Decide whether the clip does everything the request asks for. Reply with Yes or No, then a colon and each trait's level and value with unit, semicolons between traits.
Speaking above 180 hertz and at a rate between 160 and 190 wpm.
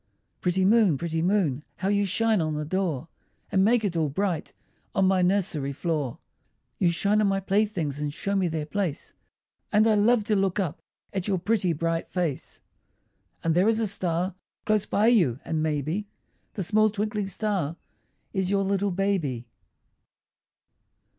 Yes: high, 190 Hz; average, 165 wpm